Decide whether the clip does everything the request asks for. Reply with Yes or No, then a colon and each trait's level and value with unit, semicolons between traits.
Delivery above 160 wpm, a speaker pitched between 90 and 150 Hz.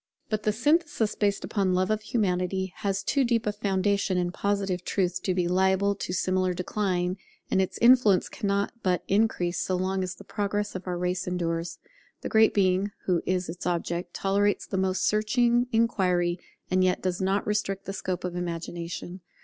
No: average, 180 wpm; high, 190 Hz